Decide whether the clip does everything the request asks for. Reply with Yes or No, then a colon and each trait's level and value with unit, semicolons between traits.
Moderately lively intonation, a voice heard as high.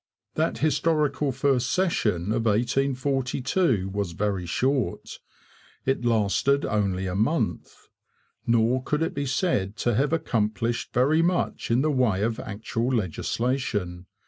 No: average, 5.0 semitones; low, 120 Hz